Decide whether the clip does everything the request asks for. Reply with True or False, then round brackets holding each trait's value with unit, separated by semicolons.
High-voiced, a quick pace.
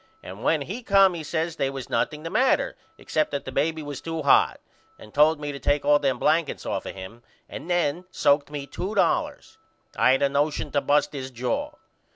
False (145 Hz; 210 wpm)